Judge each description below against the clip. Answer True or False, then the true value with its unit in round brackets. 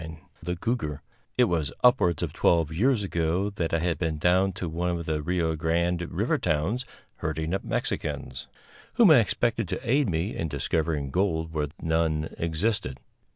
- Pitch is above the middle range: False (85 Hz)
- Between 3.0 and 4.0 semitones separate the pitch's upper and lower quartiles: True (3.4 semitones)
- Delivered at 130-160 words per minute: False (170 wpm)